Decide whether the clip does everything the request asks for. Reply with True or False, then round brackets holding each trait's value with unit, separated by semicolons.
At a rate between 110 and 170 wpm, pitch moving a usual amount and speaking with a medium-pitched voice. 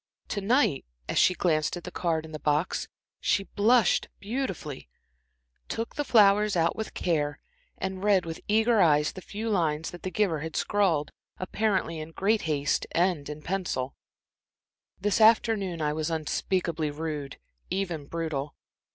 True (150 wpm; 5.0 semitones; 175 Hz)